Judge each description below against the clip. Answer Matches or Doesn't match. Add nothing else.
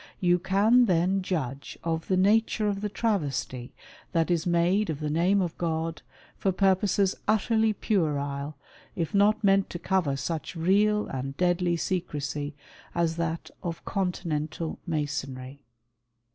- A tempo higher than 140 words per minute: Doesn't match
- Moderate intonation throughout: Matches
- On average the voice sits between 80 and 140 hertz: Doesn't match